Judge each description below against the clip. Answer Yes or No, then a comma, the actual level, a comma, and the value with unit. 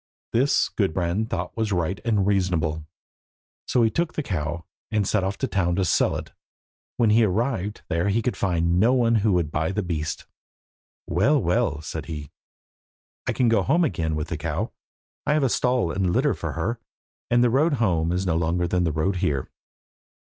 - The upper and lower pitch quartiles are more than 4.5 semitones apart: Yes, average, 5.2 semitones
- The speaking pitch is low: Yes, very low, 95 Hz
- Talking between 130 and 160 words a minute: No, average, 190 wpm